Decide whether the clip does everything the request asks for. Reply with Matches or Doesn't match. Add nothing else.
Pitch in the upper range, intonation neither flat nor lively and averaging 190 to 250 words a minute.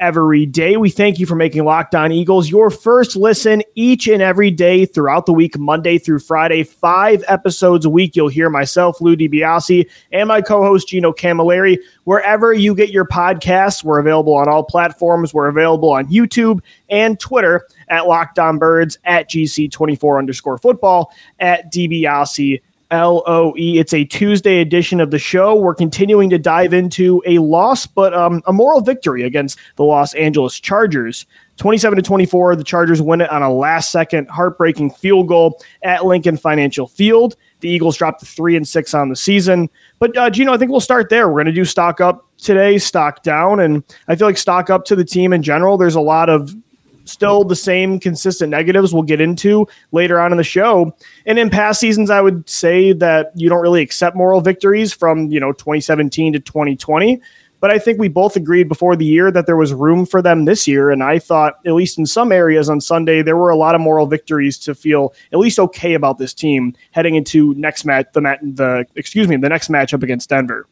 Doesn't match